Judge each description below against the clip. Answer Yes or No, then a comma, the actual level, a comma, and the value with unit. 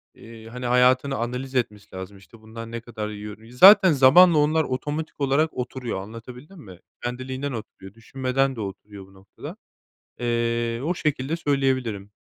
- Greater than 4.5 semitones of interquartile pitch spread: No, average, 3.5 semitones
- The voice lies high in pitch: No, low, 125 Hz